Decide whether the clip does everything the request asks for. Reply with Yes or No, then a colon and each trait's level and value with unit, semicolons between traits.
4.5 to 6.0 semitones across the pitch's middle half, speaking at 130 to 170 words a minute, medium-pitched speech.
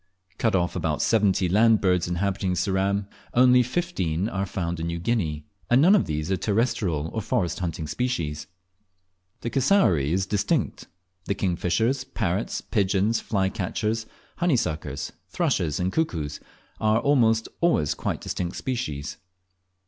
No: average, 5.1 semitones; slow, 135 wpm; very low, 95 Hz